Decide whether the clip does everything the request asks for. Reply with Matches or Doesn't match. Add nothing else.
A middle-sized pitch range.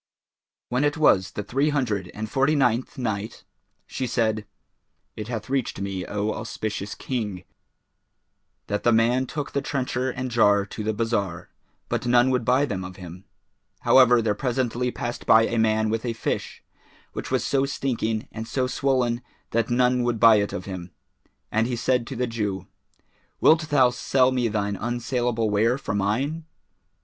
Matches